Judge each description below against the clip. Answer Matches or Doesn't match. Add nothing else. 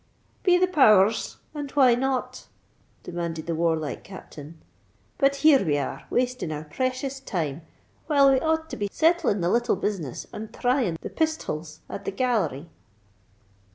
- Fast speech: Doesn't match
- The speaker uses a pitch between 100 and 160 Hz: Doesn't match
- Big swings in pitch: Matches